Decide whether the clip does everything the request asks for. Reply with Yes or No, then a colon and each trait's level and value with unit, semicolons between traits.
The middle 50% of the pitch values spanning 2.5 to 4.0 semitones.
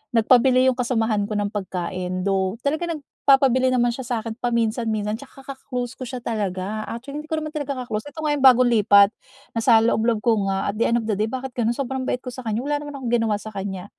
Yes: average, 3.7 semitones